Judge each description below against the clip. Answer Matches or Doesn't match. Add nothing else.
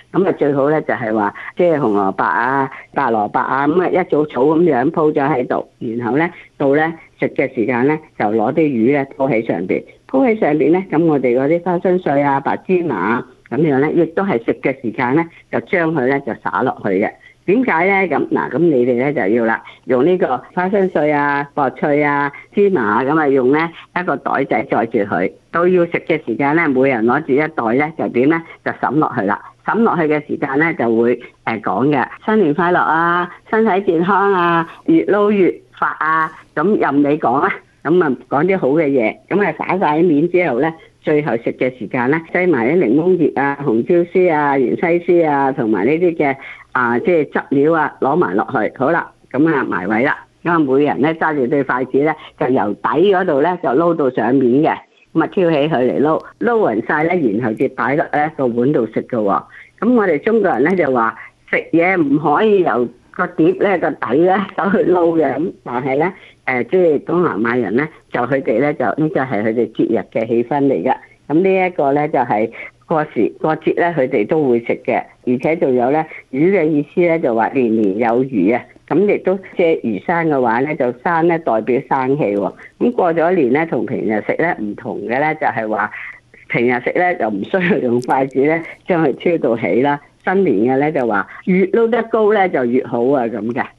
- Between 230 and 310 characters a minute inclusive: Matches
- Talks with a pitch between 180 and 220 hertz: Doesn't match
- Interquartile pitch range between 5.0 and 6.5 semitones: Matches